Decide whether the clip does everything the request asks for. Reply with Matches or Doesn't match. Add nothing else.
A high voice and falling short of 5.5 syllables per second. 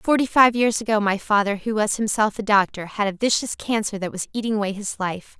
Doesn't match